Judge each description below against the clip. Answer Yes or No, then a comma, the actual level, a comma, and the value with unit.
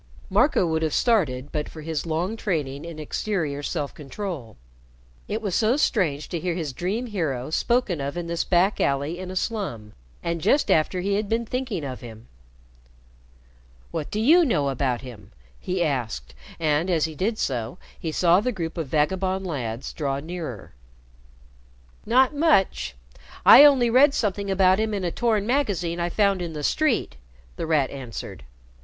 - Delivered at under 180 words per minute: Yes, average, 170 wpm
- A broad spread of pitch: Yes, wide, 6.4 semitones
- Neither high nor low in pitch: Yes, medium, 170 Hz